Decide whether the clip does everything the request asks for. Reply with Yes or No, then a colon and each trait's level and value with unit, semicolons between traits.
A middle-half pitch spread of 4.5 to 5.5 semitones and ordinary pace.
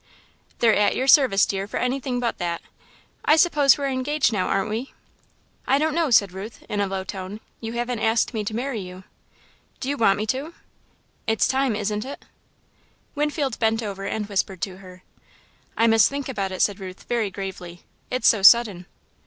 Yes: average, 5.0 semitones; average, 185 wpm